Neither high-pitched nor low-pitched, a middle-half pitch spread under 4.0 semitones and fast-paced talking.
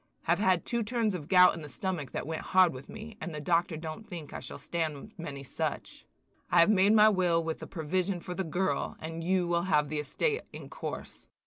Yes: medium, 175 Hz; average, 3.2 semitones; fast, 225 wpm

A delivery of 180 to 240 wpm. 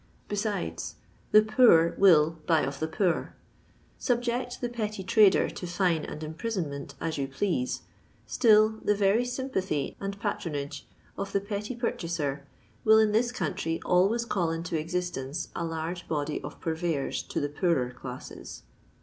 No: average, 150 wpm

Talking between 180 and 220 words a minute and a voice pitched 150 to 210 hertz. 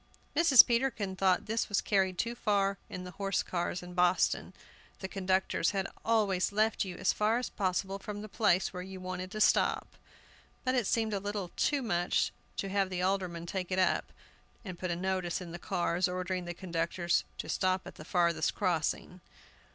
Yes: average, 190 wpm; high, 190 Hz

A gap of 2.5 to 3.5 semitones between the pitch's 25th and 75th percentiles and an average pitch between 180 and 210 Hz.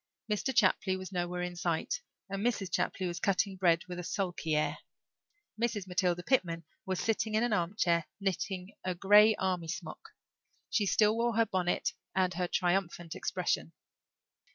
Yes: average, 2.9 semitones; medium, 185 Hz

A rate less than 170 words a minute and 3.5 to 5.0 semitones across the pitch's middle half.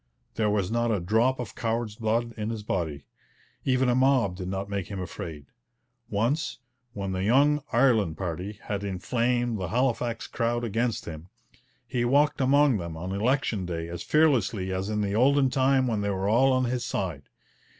No: average, 180 wpm; average, 4.6 semitones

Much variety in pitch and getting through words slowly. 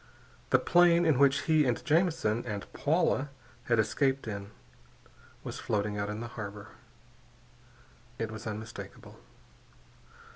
Yes: wide, 5.9 semitones; slow, 120 wpm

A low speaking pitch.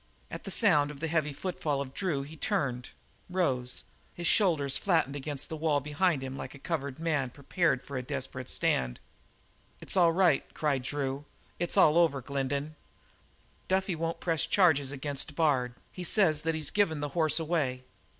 No: medium, 150 Hz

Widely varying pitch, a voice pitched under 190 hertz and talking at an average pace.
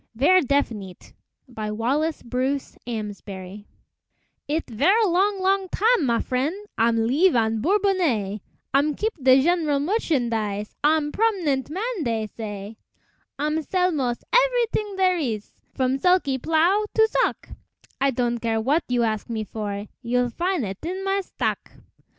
No: wide, 8.3 semitones; very high, 275 Hz; average, 145 wpm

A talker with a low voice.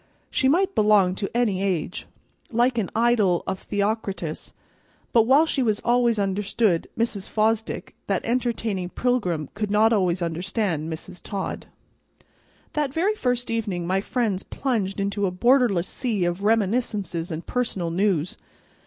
No: high, 210 Hz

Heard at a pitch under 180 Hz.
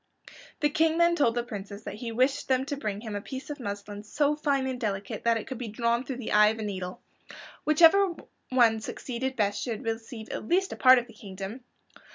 No: high, 235 Hz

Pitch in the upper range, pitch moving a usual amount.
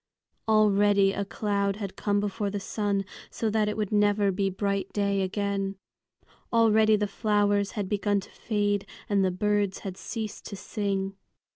No: high, 205 Hz; narrow, 1.0 semitones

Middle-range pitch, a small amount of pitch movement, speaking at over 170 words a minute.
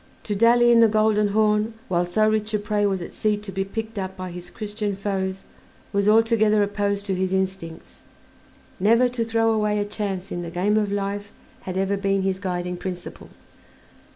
No: high, 205 Hz; narrow, 2.1 semitones; average, 190 wpm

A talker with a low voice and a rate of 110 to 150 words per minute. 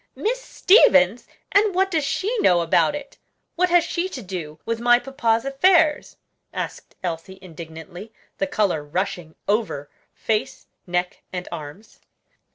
No: high, 220 Hz; average, 140 wpm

